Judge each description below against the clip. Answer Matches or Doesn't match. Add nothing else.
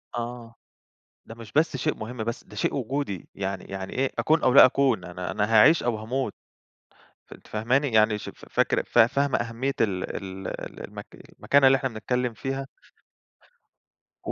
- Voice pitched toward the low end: Matches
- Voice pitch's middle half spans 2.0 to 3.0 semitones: Doesn't match